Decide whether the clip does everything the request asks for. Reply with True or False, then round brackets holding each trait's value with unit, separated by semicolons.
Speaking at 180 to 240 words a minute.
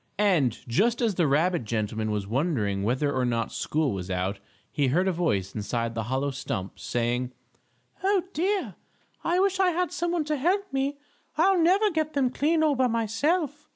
True (185 wpm)